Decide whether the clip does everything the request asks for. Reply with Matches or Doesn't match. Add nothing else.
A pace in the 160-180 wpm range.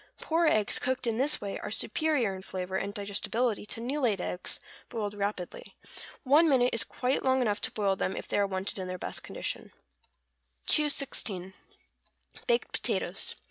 Matches